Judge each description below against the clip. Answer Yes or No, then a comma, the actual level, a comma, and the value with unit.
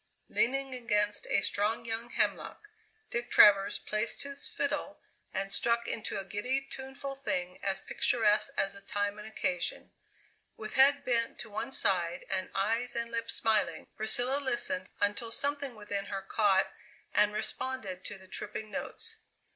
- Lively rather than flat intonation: No, average, 3.7 semitones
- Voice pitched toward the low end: No, high, 215 Hz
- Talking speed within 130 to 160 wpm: Yes, average, 150 wpm